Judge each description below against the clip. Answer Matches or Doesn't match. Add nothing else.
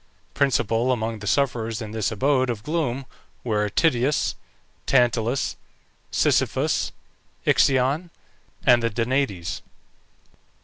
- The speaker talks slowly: Matches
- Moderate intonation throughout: Matches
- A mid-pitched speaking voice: Doesn't match